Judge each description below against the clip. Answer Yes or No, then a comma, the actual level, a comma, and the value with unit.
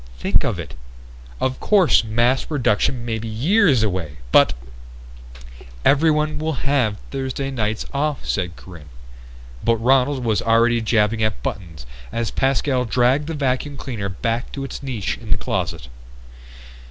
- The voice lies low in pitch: Yes, low, 120 Hz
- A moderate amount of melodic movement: Yes, average, 4.3 semitones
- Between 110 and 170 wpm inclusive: Yes, average, 145 wpm